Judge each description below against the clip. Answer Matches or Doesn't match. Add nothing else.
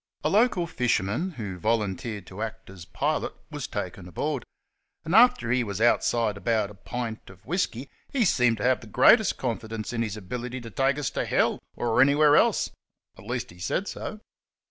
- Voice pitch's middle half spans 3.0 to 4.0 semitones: Doesn't match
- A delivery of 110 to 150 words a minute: Doesn't match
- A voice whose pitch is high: Doesn't match